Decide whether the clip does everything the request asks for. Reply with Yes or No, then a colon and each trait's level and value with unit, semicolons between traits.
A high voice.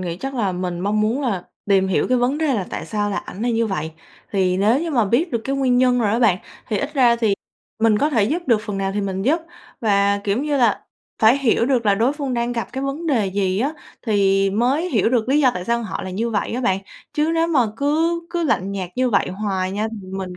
Yes: high, 225 Hz